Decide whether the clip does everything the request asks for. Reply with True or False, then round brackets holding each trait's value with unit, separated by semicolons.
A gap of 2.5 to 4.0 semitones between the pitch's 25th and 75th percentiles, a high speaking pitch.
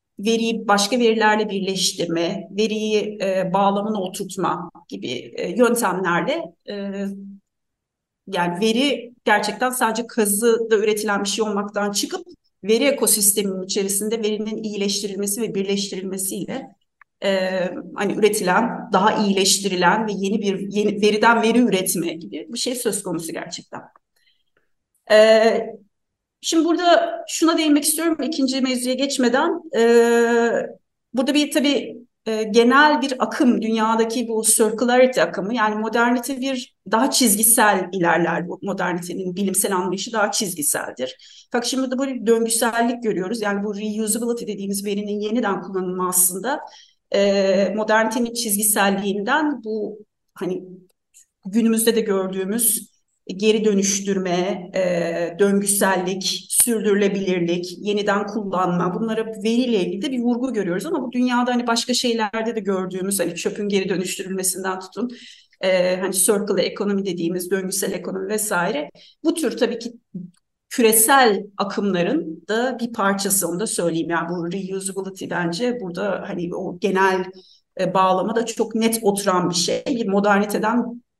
True (3.4 semitones; 210 Hz)